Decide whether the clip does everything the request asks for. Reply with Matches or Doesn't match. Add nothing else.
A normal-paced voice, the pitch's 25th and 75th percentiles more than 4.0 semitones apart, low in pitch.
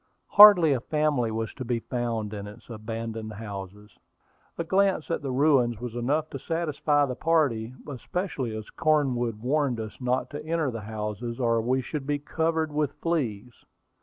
Matches